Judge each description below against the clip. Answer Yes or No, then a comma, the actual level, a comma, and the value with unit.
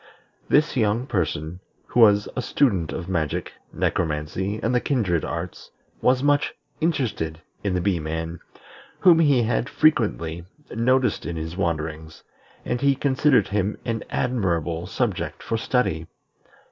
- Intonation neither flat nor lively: No, wide, 7.2 semitones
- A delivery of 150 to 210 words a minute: No, slow, 135 wpm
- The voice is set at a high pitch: No, low, 100 Hz